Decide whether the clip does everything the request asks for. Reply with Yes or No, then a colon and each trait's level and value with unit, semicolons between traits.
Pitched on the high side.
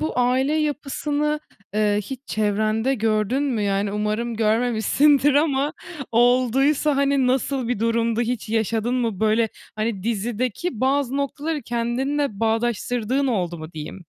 Yes: high, 240 Hz